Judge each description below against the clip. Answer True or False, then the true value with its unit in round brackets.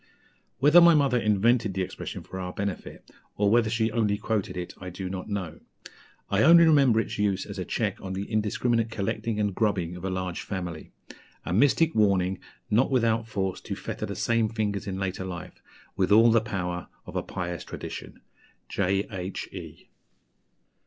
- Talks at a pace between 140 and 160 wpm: False (175 wpm)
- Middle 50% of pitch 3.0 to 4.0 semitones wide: True (3.3 semitones)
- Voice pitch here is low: True (100 Hz)